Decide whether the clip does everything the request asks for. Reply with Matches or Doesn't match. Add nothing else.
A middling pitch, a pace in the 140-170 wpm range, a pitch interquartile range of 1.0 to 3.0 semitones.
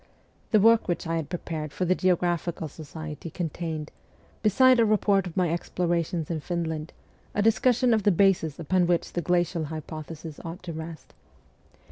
Matches